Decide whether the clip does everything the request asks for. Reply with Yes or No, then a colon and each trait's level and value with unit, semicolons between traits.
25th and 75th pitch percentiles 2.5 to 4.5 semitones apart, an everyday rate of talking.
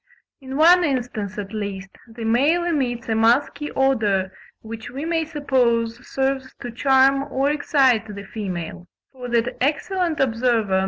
Yes: average, 3.8 semitones; average, 160 wpm